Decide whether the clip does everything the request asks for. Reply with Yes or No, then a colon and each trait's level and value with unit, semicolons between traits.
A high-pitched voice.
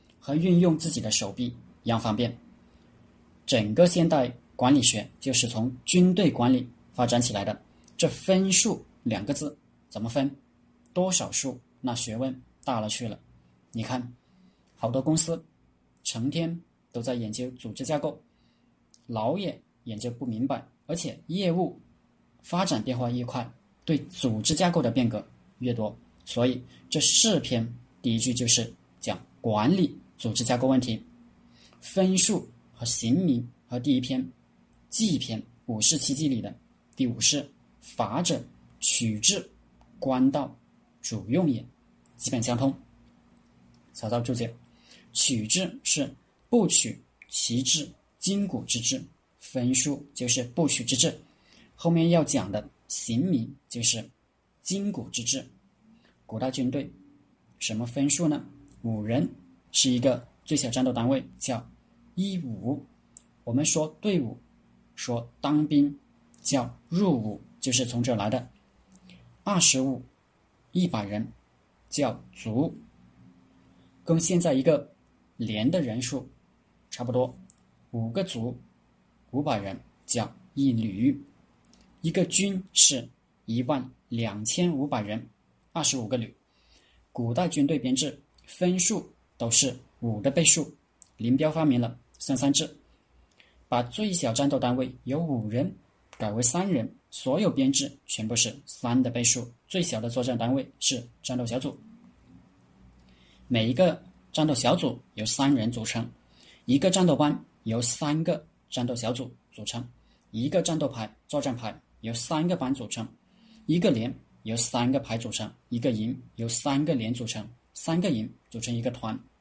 No: low, 125 Hz